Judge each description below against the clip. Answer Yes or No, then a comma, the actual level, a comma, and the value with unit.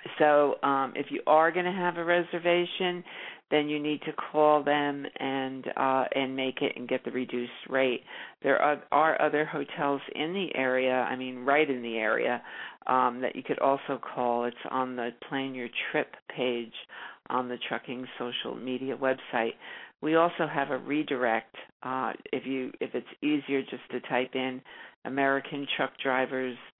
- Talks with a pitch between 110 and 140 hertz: Yes, low, 135 Hz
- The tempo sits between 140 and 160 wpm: No, average, 170 wpm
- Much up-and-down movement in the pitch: No, average, 2.7 semitones